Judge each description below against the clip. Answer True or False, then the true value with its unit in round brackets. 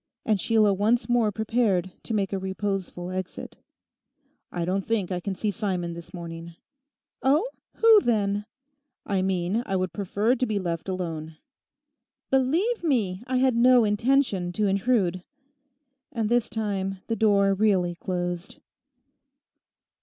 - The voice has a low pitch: False (200 Hz)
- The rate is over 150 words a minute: False (140 wpm)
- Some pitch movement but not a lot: True (4.0 semitones)